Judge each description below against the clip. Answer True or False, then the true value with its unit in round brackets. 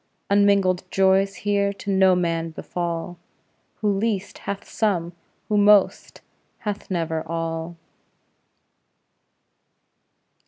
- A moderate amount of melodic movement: True (3.0 semitones)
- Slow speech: True (90 wpm)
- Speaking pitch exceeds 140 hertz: True (190 Hz)